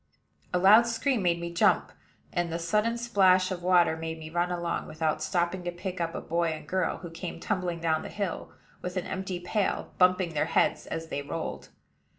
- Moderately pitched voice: Yes, medium, 175 Hz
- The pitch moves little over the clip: Yes, narrow, 2.1 semitones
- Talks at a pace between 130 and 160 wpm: No, average, 200 wpm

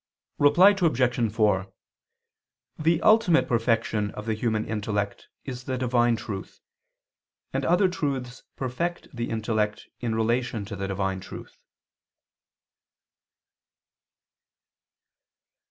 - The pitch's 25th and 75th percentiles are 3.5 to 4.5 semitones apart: Yes, average, 3.8 semitones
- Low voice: Yes, low, 120 Hz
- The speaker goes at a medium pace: No, slow, 100 wpm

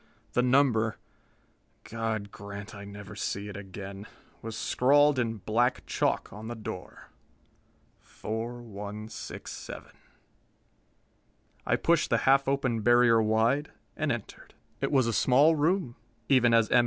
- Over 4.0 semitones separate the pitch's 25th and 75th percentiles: No, average, 3.5 semitones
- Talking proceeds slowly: Yes, slow, 125 wpm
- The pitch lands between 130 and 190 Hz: No, low, 115 Hz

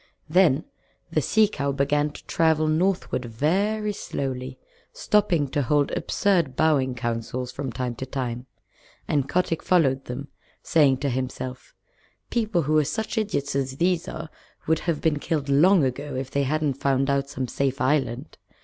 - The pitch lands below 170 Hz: Yes, medium, 140 Hz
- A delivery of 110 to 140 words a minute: No, average, 160 wpm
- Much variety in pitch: No, average, 3.7 semitones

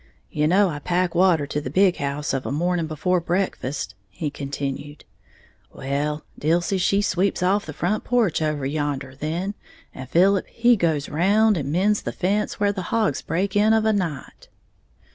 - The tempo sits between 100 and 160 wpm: No, average, 175 wpm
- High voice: No, medium, 175 Hz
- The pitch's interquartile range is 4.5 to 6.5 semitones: Yes, average, 5.1 semitones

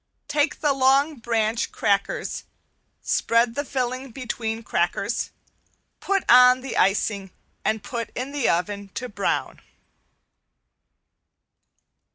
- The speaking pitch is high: Yes, high, 245 Hz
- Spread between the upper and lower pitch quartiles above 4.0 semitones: No, average, 3.6 semitones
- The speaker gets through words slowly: Yes, slow, 110 wpm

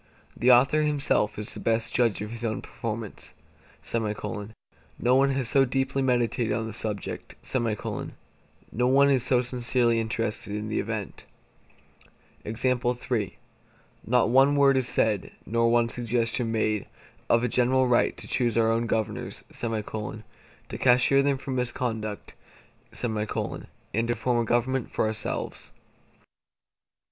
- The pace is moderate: No, slow, 130 wpm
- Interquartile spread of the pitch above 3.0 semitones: No, narrow, 2.4 semitones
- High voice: No, low, 120 Hz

